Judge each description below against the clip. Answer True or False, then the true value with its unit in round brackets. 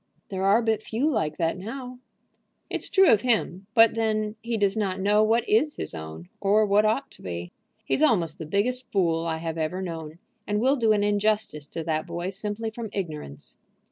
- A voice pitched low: False (205 Hz)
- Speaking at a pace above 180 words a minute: True (200 wpm)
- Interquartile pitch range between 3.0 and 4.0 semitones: False (5.2 semitones)